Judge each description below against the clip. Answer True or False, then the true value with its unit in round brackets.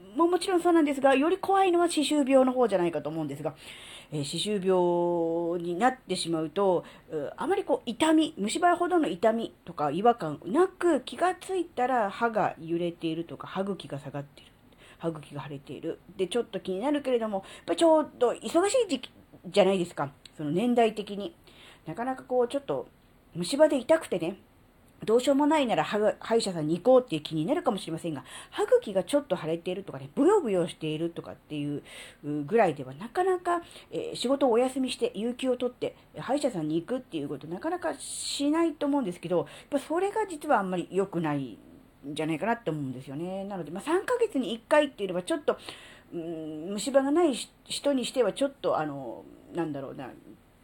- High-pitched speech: True (210 Hz)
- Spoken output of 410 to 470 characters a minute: True (415 characters per minute)